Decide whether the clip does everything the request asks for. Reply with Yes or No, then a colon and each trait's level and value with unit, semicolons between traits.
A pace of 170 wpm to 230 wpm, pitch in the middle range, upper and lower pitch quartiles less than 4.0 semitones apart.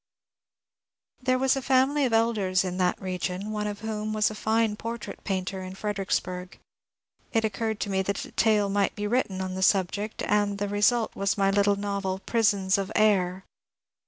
No: average, 190 wpm; high, 205 Hz; narrow, 2.4 semitones